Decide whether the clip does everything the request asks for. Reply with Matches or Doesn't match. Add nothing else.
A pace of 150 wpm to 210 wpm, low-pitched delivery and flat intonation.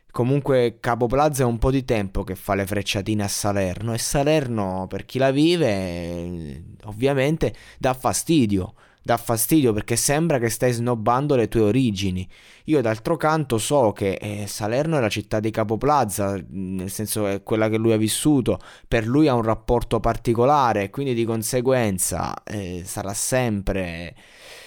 Doesn't match